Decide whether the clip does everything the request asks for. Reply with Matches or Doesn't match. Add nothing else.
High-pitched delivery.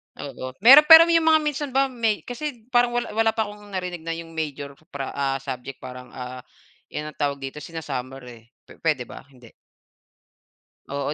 Doesn't match